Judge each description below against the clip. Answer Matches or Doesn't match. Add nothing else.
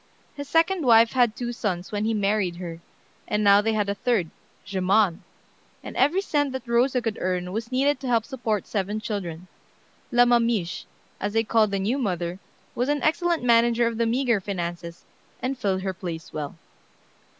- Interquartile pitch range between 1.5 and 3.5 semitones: Doesn't match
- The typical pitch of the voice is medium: Doesn't match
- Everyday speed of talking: Matches